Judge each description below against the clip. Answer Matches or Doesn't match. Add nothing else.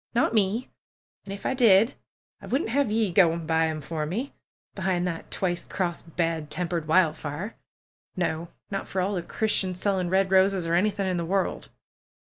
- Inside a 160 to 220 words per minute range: Matches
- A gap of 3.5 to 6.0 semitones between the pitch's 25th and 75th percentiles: Doesn't match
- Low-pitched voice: Doesn't match